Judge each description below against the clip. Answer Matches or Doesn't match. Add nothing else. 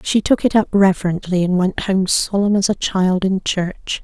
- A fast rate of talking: Matches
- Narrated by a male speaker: Doesn't match